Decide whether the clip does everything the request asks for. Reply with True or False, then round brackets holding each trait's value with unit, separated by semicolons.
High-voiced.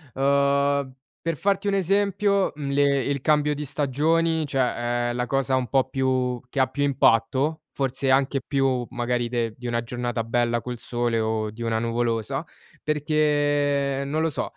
False (135 Hz)